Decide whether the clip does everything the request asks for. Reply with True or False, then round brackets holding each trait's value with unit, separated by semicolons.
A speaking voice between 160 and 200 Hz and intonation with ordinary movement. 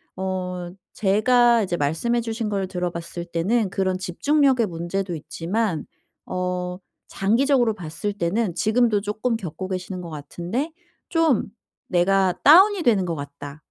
True (190 Hz; 4.8 semitones)